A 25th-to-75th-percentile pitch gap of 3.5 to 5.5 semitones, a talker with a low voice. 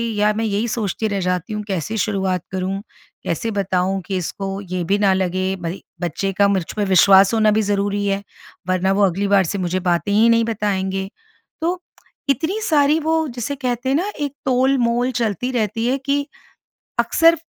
No: average, 4.2 semitones; high, 205 Hz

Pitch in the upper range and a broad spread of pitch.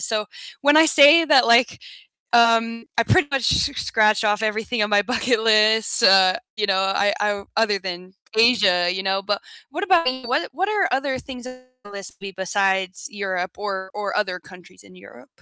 No: high, 215 Hz; average, 4.6 semitones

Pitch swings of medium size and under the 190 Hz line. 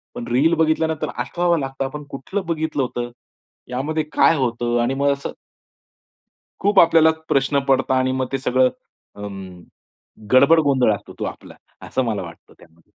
Yes: average, 4.6 semitones; low, 135 Hz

